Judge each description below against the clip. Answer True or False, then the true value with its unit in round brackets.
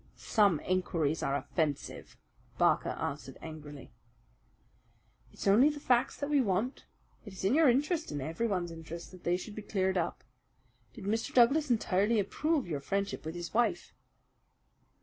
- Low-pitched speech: False (195 Hz)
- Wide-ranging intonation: True (6.1 semitones)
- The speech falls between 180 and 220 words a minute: False (150 wpm)